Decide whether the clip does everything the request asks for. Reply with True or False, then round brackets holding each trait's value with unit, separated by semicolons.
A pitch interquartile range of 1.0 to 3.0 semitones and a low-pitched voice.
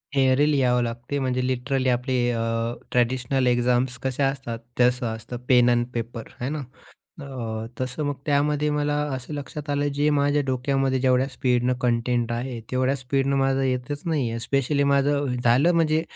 True (2.4 semitones; 130 Hz)